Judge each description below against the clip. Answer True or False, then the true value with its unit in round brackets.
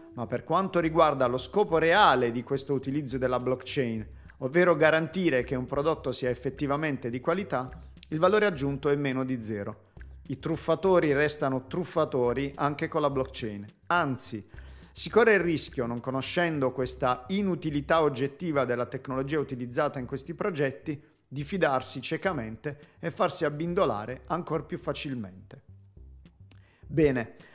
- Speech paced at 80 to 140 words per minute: True (135 wpm)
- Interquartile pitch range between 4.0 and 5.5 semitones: True (4.4 semitones)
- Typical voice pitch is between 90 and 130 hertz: False (140 Hz)